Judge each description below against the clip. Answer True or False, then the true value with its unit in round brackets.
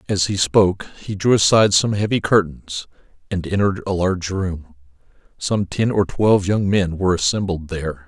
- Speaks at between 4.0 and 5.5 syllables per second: True (5.4 syllables/s)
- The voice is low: True (95 Hz)